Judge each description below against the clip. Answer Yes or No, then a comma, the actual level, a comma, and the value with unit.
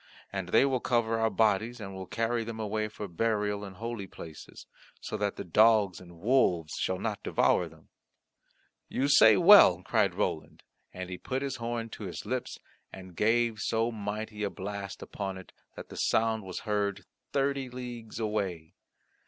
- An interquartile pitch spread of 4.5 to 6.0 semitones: No, average, 2.9 semitones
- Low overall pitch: Yes, low, 110 Hz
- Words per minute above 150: Yes, average, 175 wpm